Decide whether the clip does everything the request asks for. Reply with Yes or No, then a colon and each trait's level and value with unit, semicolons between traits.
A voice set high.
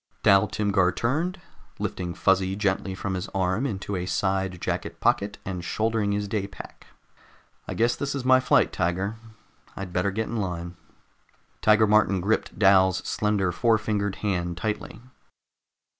No: low, 100 Hz